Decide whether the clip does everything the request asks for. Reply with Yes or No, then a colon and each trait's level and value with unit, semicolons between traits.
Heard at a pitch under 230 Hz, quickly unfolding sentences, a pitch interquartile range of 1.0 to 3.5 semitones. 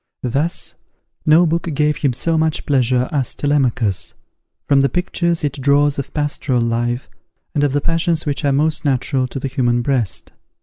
No: medium, 140 Hz; average, 170 wpm; average, 3.1 semitones